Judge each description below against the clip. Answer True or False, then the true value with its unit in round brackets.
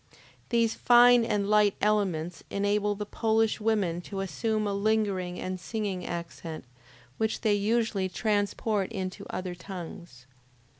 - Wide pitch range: False (3.0 semitones)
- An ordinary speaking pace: False (130 wpm)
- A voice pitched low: False (205 Hz)